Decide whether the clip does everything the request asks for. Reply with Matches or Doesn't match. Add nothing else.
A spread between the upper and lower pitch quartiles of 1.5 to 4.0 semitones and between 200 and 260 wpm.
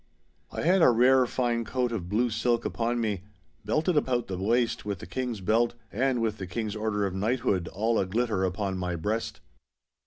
Doesn't match